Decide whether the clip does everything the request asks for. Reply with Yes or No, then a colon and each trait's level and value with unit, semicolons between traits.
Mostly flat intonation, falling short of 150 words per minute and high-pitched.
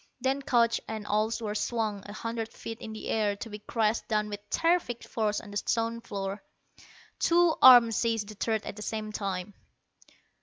No: narrow, 1.8 semitones; average, 185 wpm; high, 220 Hz